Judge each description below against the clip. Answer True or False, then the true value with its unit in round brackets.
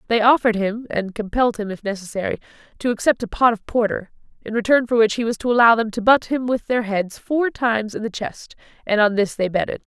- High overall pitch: True (225 Hz)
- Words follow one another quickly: True (235 wpm)